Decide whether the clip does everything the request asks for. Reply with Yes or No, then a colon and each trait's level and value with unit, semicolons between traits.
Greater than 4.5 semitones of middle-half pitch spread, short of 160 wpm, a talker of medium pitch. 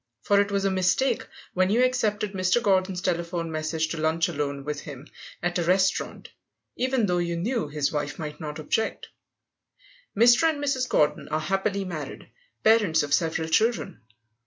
No: average, 4.9 semitones; average, 165 wpm; medium, 180 Hz